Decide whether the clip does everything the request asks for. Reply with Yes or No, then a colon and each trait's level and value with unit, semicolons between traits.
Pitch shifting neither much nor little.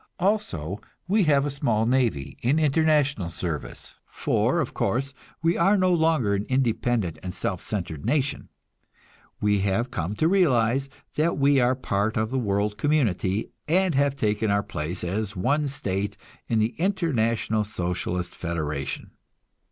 No: wide, 6.6 semitones